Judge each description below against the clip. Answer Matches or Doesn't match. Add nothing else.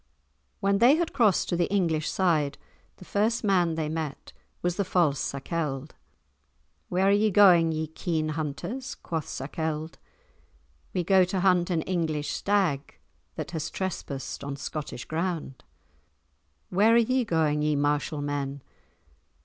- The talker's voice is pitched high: Doesn't match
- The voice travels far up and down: Doesn't match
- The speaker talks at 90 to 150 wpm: Matches